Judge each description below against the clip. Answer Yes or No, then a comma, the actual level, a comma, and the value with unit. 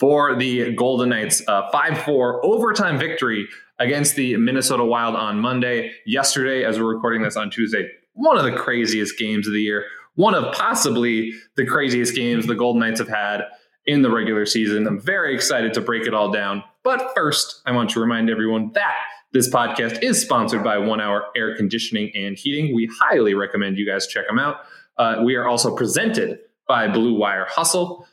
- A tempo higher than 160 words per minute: Yes, average, 190 wpm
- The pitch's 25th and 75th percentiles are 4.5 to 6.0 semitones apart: No, average, 3.2 semitones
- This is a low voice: Yes, low, 115 Hz